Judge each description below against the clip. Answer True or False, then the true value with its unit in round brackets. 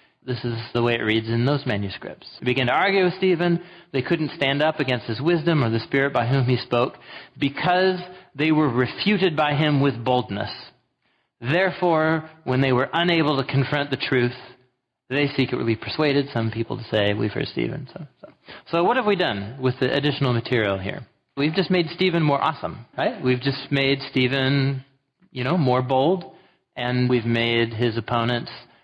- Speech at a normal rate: True (185 wpm)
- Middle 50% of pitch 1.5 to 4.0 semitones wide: False (4.4 semitones)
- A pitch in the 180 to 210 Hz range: False (135 Hz)